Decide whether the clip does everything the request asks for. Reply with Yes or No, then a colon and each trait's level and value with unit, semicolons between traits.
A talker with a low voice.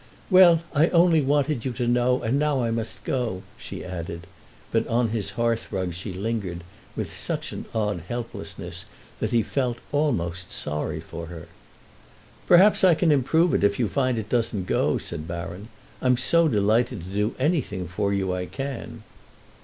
Yes: low, 115 Hz